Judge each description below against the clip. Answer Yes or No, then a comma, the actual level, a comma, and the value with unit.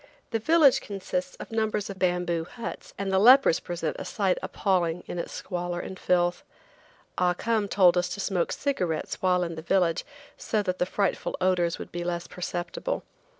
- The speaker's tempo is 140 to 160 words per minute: No, average, 180 wpm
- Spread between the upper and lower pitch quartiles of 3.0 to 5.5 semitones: No, narrow, 2.5 semitones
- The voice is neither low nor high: Yes, medium, 180 Hz